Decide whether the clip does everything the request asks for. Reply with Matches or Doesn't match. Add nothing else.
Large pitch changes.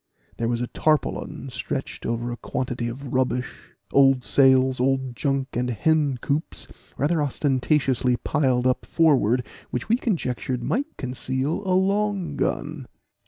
Doesn't match